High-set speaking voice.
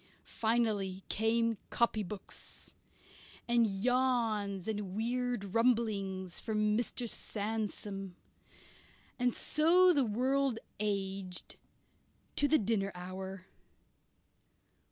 Yes: high, 220 Hz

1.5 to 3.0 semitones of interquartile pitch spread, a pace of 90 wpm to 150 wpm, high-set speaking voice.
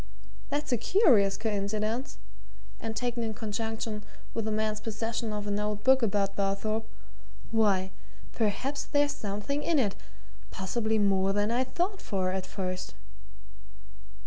Yes: average, 2.7 semitones; slow, 135 wpm; high, 215 Hz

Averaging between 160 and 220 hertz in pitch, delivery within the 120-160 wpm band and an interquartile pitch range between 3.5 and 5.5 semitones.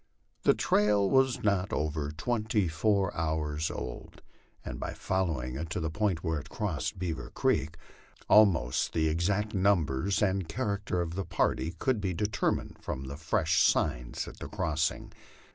No: very low, 85 Hz; average, 155 wpm; average, 4.5 semitones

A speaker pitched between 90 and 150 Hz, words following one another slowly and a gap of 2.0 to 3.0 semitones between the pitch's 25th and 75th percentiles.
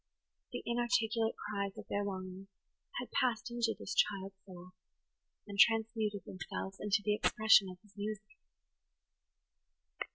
No: high, 210 Hz; slow, 125 wpm; narrow, 2.4 semitones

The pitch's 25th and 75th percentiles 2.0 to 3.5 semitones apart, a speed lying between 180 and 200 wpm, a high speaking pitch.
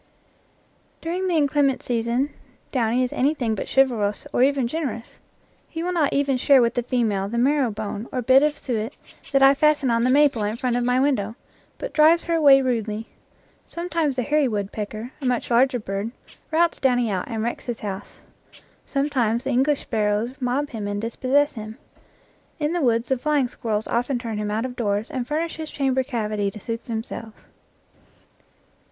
No: average, 4.0 semitones; average, 185 wpm; very high, 250 Hz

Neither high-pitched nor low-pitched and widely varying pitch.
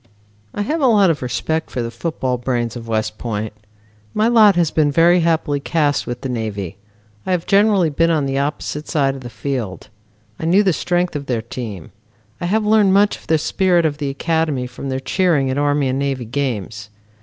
Yes: medium, 145 Hz; wide, 5.8 semitones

